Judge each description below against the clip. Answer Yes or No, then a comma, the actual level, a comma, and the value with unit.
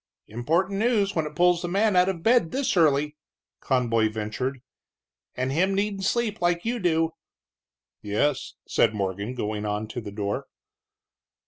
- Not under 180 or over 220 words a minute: No, average, 150 wpm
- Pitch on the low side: No, medium, 160 Hz